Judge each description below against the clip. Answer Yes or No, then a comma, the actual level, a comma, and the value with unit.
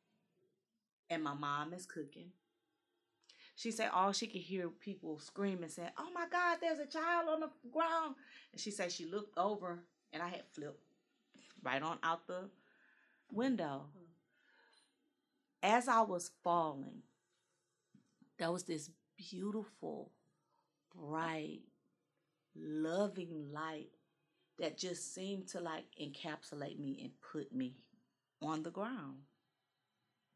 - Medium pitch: Yes, medium, 180 Hz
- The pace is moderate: No, slow, 125 wpm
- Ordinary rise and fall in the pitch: No, wide, 5.7 semitones